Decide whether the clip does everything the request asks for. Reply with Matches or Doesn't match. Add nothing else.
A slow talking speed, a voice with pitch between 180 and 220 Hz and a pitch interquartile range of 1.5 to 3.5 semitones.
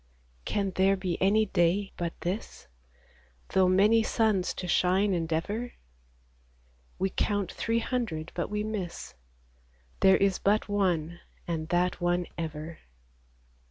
Matches